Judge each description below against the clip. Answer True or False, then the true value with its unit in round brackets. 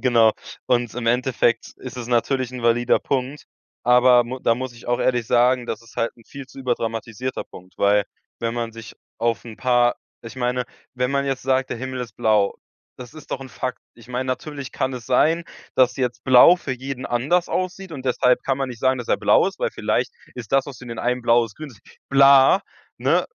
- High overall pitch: False (125 Hz)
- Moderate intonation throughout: False (1.9 semitones)